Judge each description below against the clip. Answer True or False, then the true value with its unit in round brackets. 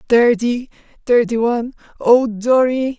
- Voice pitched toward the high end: True (240 Hz)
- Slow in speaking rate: True (80 wpm)